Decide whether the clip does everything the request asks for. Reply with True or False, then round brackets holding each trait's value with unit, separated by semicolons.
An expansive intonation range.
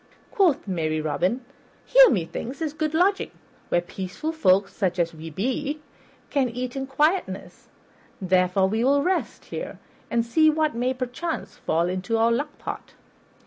True (8.4 semitones)